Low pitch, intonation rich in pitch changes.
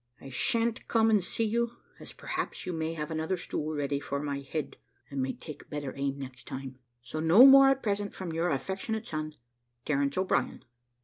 No: medium, 160 Hz; wide, 6.7 semitones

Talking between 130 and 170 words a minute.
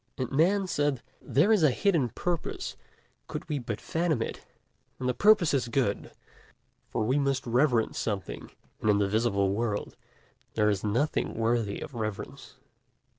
Yes: average, 155 wpm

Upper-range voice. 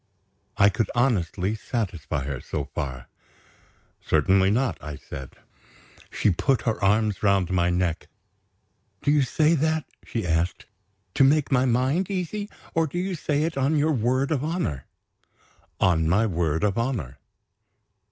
No: low, 110 Hz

